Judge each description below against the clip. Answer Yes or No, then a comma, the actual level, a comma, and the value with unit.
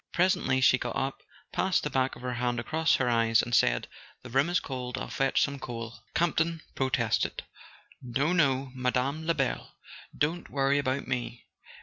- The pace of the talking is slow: No, average, 165 wpm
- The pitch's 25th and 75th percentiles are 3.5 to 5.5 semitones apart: No, average, 3.1 semitones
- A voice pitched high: No, low, 130 Hz